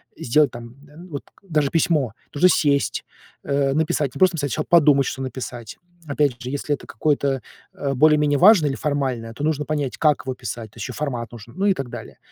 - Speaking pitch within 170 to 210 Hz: No, medium, 140 Hz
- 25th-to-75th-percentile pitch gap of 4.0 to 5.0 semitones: No, average, 3.1 semitones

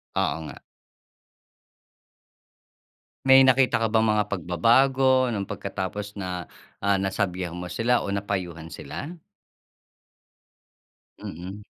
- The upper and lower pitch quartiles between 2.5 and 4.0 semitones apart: No, average, 4.9 semitones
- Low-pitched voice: Yes, low, 100 Hz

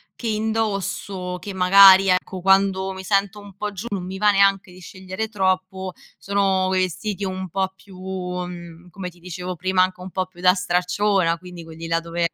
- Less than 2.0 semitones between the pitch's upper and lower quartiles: Yes, narrow, 1.5 semitones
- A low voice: No, medium, 185 Hz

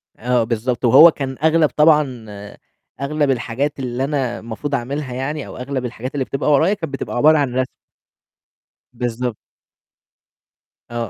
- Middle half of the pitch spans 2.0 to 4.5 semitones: Yes, average, 3.2 semitones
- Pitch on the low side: Yes, low, 130 Hz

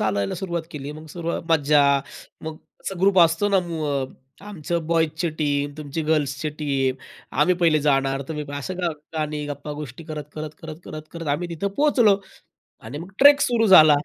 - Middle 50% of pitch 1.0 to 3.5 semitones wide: Yes, average, 3.0 semitones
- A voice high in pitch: No, medium, 155 Hz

